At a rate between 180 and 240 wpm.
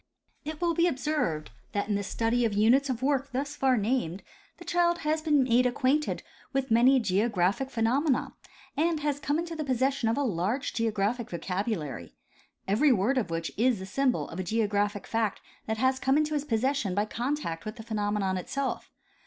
Yes: average, 185 wpm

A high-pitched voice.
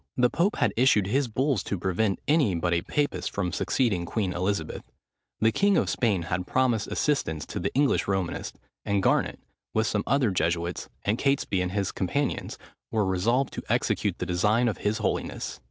No: low, 105 Hz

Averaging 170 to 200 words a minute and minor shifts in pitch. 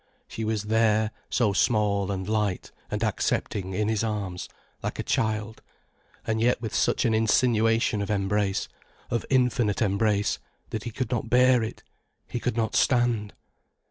No: average, 155 wpm; narrow, 1.9 semitones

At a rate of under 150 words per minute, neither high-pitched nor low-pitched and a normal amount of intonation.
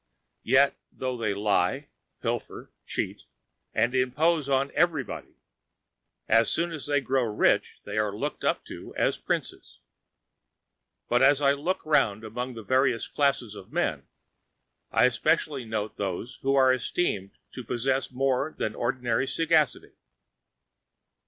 No: slow, 135 wpm; low, 130 Hz; average, 3.6 semitones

